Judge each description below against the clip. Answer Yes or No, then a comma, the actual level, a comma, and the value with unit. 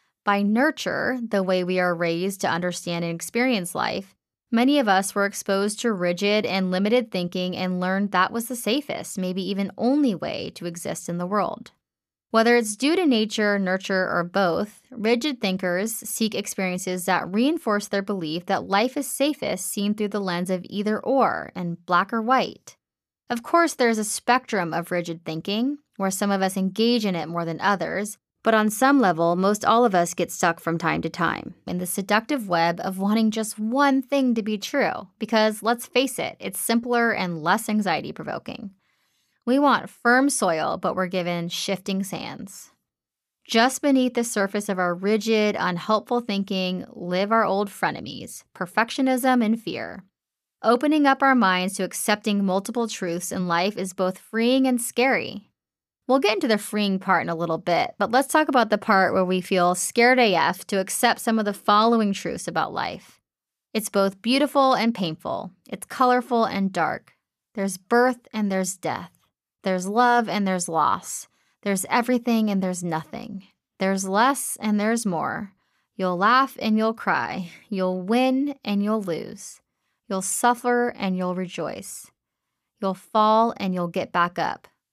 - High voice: Yes, high, 205 Hz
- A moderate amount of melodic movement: Yes, average, 4.3 semitones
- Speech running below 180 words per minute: Yes, average, 170 wpm